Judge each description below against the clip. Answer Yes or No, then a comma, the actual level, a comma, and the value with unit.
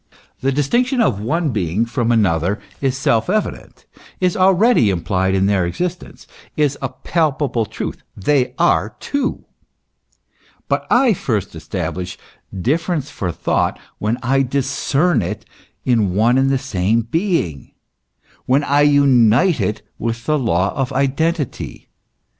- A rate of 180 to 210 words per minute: No, slow, 135 wpm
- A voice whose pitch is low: Yes, low, 130 Hz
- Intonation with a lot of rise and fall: Yes, wide, 6.4 semitones